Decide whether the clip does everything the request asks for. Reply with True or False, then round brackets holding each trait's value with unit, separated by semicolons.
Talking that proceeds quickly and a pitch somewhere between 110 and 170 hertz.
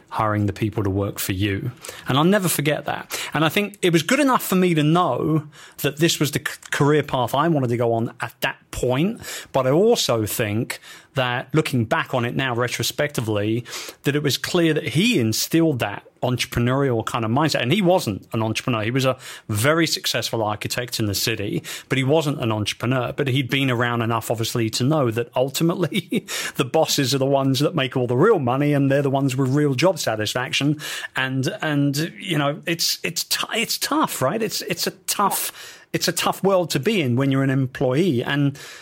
True (220 wpm; 135 Hz)